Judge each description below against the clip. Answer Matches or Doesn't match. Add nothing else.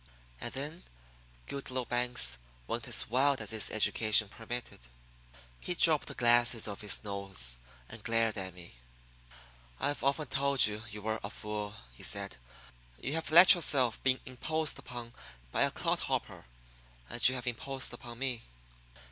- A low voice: Matches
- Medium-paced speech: Matches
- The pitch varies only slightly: Doesn't match